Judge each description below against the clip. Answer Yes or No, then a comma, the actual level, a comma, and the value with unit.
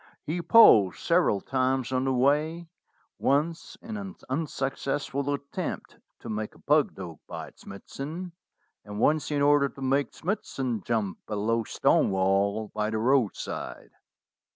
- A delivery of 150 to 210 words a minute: No, average, 140 wpm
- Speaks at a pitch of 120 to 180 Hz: Yes, low, 135 Hz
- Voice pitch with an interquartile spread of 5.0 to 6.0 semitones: Yes, wide, 5.5 semitones